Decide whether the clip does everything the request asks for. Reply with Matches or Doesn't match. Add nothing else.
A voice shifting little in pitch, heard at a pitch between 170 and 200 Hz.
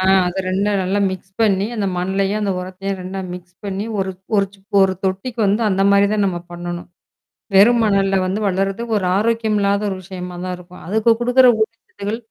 Matches